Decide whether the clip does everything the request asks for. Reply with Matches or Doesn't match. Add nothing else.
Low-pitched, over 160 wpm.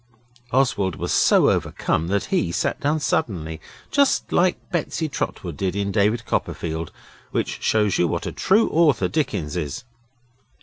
Doesn't match